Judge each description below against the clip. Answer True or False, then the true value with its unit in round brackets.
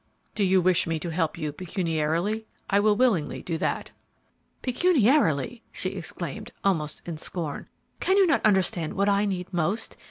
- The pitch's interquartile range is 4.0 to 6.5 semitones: True (4.7 semitones)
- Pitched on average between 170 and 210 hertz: True (185 Hz)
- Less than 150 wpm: False (155 wpm)